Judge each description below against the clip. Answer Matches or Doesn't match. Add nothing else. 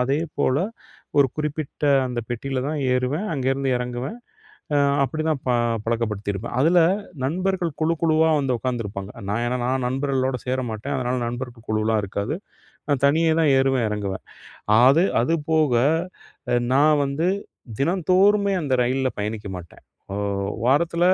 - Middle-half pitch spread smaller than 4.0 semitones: Doesn't match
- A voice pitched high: Doesn't match